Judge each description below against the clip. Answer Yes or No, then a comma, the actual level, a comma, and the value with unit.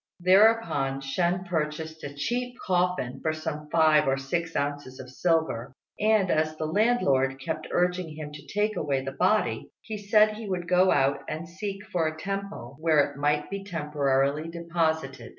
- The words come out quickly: No, average, 170 wpm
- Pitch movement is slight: No, average, 4.3 semitones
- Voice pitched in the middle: Yes, medium, 160 Hz